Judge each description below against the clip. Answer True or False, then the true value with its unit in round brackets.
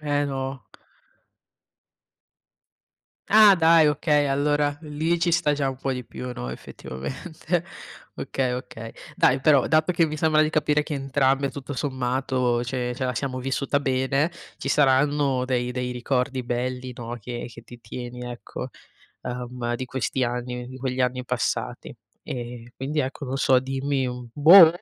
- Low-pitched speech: True (130 Hz)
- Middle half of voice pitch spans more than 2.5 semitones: True (2.9 semitones)